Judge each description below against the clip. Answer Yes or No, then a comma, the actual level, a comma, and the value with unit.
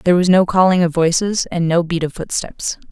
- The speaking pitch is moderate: Yes, medium, 175 Hz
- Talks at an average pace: No, fast, 225 wpm